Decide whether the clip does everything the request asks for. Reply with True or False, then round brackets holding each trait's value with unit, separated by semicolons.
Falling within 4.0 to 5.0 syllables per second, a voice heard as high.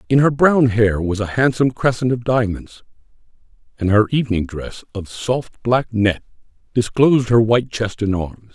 False (4.9 syllables/s; 115 Hz)